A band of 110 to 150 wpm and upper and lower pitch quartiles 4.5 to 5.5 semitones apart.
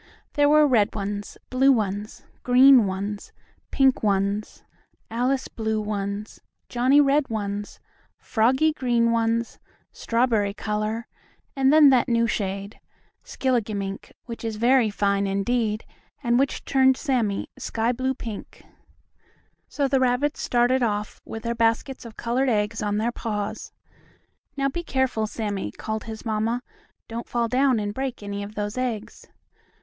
No: average, 140 wpm; average, 3.7 semitones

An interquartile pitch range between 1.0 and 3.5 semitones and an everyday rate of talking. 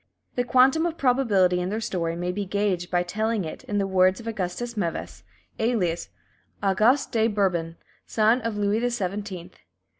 No: average, 4.1 semitones; average, 170 wpm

